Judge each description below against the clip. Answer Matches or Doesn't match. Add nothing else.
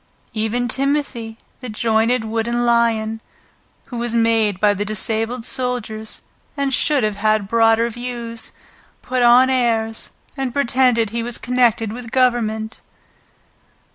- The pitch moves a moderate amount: Doesn't match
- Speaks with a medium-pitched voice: Doesn't match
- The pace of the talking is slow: Matches